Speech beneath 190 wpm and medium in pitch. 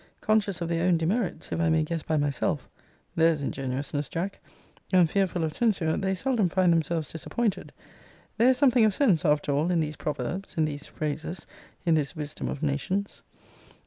Yes: average, 175 wpm; medium, 165 Hz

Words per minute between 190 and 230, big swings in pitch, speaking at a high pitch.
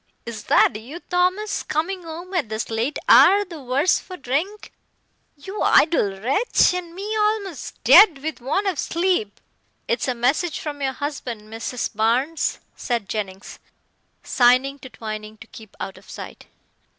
No: average, 150 wpm; wide, 7.8 semitones; very high, 285 Hz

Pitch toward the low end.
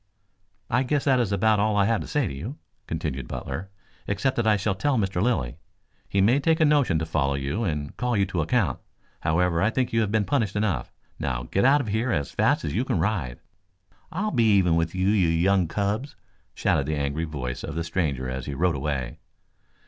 Yes: very low, 95 Hz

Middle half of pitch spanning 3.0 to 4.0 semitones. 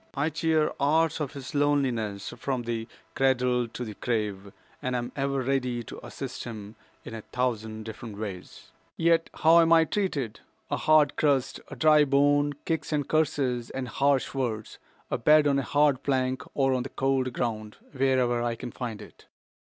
Yes: average, 3.4 semitones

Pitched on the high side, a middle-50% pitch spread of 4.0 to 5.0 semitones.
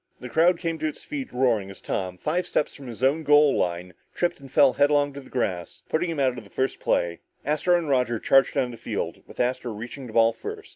No: low, 135 Hz; average, 4.6 semitones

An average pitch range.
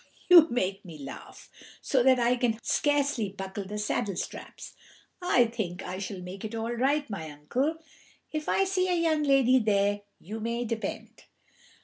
No: wide, 5.9 semitones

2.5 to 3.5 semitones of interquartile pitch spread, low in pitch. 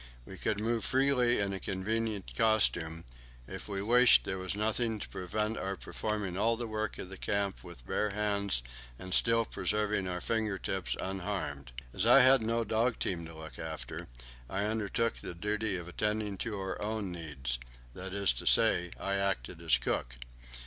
Yes: average, 3.1 semitones; low, 100 Hz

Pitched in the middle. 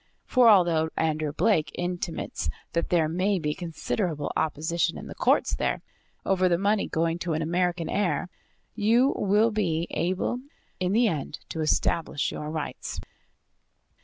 Yes: medium, 175 Hz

